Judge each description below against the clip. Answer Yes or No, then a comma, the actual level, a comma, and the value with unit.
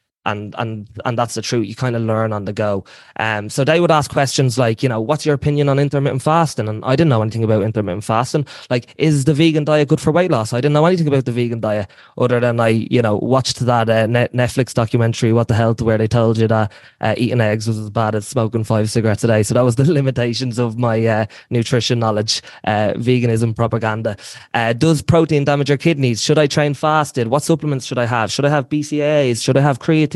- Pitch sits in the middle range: No, low, 120 Hz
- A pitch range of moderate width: Yes, average, 4.4 semitones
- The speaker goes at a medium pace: No, fast, 235 wpm